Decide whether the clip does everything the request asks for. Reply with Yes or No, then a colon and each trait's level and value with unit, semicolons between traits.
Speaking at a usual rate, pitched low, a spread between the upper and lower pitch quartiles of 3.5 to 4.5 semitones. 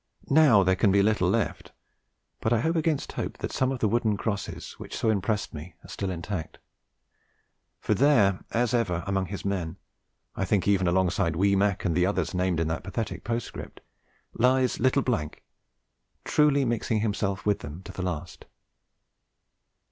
Yes: average, 170 wpm; low, 100 Hz; average, 4.0 semitones